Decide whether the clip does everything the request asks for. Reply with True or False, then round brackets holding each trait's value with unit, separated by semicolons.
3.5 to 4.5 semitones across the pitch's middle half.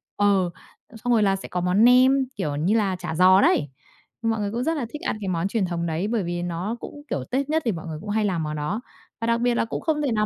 False (5.3 semitones)